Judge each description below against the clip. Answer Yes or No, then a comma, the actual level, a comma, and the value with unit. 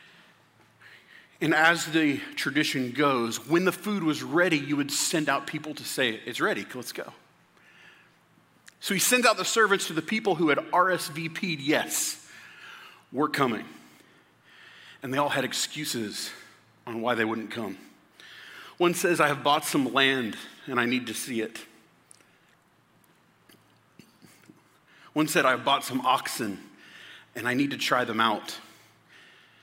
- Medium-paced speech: Yes, average, 150 wpm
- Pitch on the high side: No, medium, 150 Hz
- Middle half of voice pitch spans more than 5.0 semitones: Yes, wide, 5.6 semitones